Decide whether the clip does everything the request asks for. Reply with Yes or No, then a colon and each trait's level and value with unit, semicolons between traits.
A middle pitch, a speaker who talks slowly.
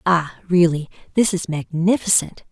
Yes: medium, 175 Hz; slow, 120 wpm